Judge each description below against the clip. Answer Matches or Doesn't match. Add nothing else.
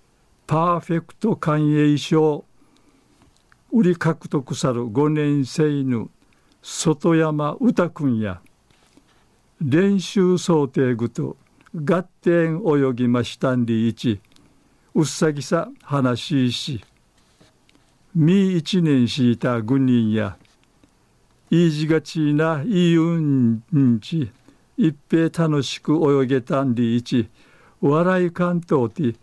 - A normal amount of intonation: Matches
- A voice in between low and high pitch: Matches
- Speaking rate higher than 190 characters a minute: Doesn't match